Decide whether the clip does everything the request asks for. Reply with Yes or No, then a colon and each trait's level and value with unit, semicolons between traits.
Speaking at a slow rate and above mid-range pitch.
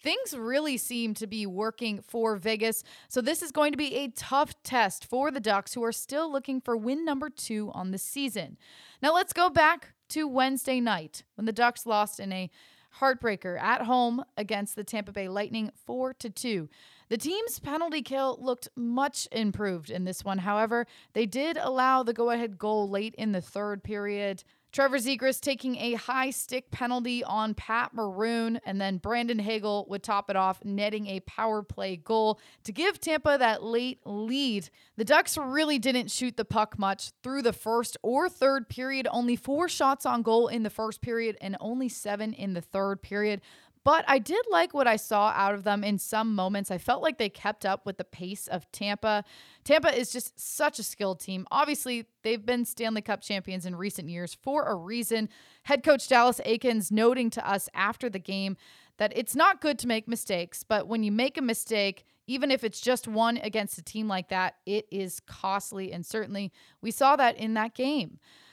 No: average, 195 wpm; high, 225 Hz